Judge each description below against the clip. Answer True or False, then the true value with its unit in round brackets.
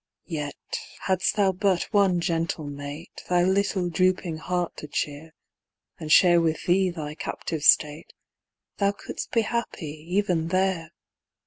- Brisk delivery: False (135 wpm)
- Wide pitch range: False (3.2 semitones)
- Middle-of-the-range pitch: True (175 Hz)